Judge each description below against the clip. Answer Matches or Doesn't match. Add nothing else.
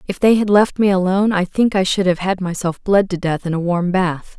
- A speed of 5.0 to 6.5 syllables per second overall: Matches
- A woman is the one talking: Matches